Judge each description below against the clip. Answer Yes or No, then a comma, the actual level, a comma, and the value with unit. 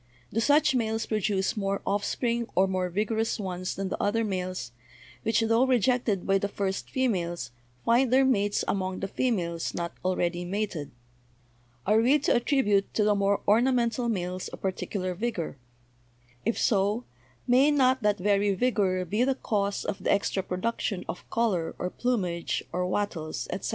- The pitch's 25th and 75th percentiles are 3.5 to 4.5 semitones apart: Yes, average, 4.0 semitones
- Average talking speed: Yes, average, 160 wpm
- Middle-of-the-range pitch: No, high, 205 Hz